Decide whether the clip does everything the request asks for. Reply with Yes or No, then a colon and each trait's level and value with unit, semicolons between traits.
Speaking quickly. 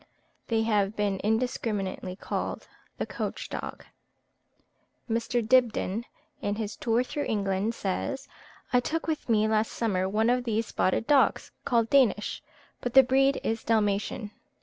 No: average, 140 wpm